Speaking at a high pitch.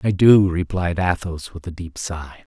No: very low, 85 Hz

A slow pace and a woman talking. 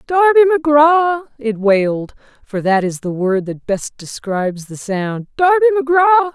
Yes: slow, 130 wpm; female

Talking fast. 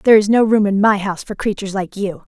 Yes: fast, 280 wpm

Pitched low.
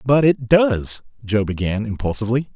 Yes: low, 120 Hz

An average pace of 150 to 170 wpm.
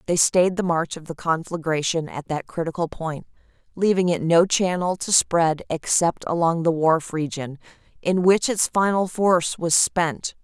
Yes: average, 165 wpm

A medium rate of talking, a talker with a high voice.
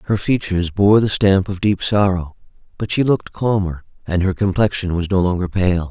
No: average, 195 wpm; very low, 95 Hz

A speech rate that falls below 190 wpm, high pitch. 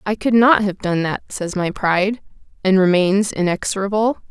Yes: average, 165 wpm; high, 195 Hz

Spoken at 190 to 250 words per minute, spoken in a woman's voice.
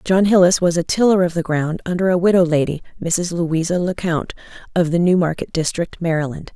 Yes: average, 200 wpm; female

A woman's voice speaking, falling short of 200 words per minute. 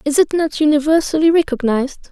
Yes: female; average, 140 wpm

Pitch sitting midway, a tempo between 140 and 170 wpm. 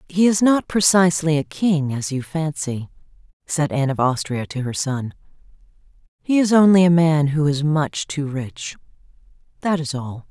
Yes: medium, 155 Hz; average, 165 wpm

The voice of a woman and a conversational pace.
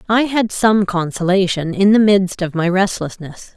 Yes: female; average, 170 wpm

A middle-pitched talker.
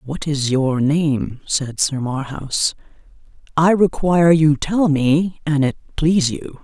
Yes: medium, 150 Hz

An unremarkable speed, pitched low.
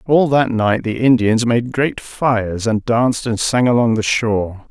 Yes: average, 190 wpm; low, 115 Hz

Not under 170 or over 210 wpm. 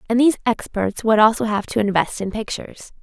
Yes: average, 200 wpm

